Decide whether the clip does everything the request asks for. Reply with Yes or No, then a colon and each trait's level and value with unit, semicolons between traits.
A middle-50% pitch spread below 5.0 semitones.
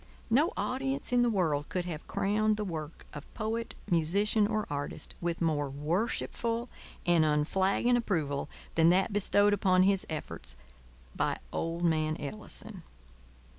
No: wide, 5.5 semitones